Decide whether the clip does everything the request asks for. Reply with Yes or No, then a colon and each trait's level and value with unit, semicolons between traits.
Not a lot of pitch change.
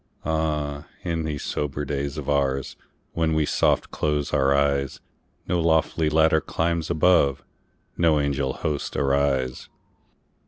Yes: narrow, 2.2 semitones